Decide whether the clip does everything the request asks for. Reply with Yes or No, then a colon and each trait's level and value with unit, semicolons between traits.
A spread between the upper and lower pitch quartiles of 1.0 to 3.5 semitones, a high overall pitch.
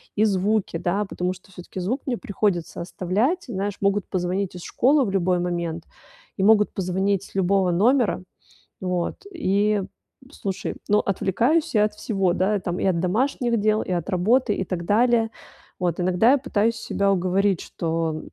Yes: average, 3.2 semitones; high, 195 Hz